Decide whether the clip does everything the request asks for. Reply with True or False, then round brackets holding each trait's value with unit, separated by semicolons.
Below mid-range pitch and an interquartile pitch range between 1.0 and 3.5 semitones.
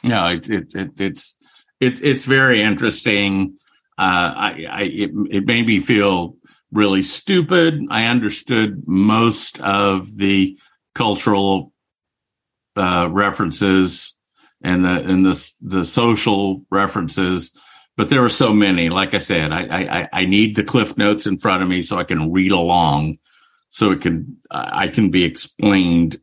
True (95 Hz; 2.5 semitones)